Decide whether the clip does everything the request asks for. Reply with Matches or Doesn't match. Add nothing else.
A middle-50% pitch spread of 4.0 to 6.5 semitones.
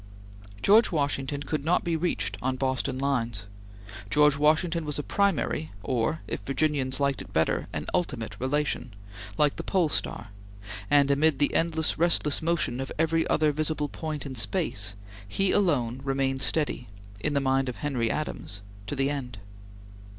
Doesn't match